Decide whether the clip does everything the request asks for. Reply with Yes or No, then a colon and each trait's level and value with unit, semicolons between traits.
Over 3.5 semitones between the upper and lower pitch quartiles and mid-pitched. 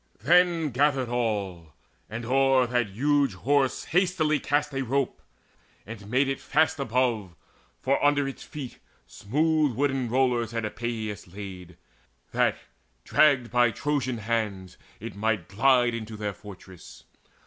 No: average, 4.5 semitones; low, 120 Hz